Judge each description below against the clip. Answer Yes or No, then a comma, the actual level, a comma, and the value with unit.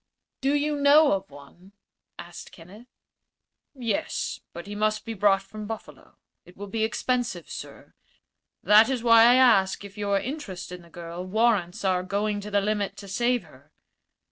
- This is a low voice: No, high, 205 Hz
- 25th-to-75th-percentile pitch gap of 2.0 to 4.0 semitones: Yes, average, 3.7 semitones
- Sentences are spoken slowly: No, average, 170 wpm